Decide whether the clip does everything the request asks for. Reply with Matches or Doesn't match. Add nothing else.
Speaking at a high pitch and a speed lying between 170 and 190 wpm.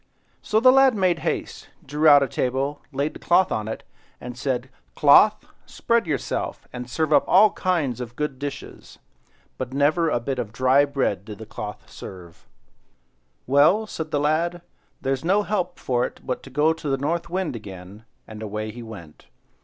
Doesn't match